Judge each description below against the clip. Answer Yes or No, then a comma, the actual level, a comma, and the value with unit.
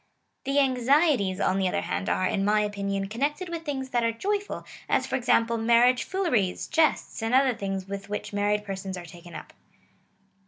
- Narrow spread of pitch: No, average, 5.3 semitones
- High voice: Yes, high, 225 Hz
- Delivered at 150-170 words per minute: No, average, 190 wpm